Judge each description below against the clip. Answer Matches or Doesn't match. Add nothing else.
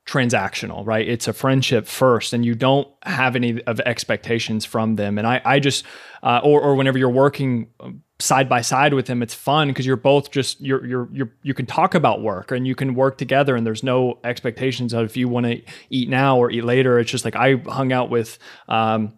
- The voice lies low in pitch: Matches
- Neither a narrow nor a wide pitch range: Doesn't match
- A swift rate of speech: Matches